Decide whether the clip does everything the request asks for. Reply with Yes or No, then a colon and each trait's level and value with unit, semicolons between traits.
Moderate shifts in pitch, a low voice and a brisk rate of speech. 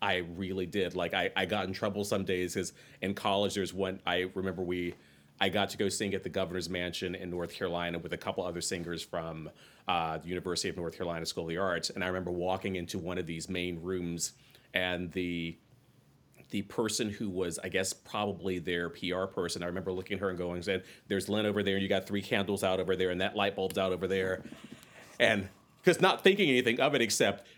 No: narrow, 2.1 semitones; very low, 95 Hz; fast, 225 wpm